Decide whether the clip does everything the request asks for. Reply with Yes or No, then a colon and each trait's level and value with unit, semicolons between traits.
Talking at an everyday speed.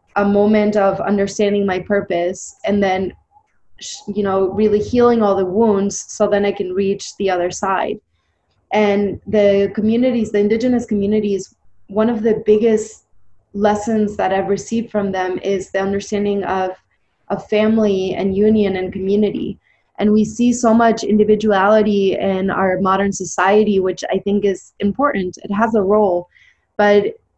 Yes: average, 150 wpm